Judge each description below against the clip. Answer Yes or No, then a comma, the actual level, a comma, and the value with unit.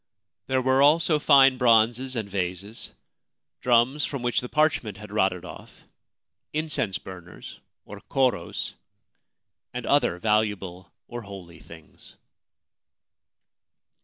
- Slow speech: Yes, slow, 105 wpm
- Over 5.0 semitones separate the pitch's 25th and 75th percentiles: Yes, wide, 5.5 semitones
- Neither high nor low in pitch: No, low, 115 Hz